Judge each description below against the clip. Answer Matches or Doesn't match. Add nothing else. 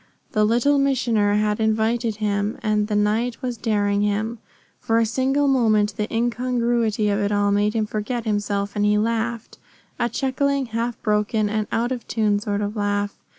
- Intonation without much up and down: Matches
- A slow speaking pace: Doesn't match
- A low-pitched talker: Doesn't match